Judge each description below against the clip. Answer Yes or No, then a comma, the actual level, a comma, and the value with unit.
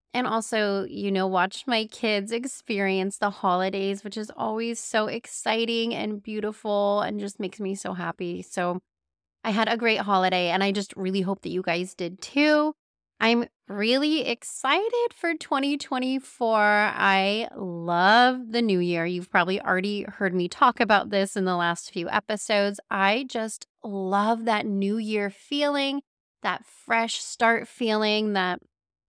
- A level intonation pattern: No, average, 3.3 semitones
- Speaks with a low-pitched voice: No, high, 210 Hz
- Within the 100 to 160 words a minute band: Yes, average, 155 wpm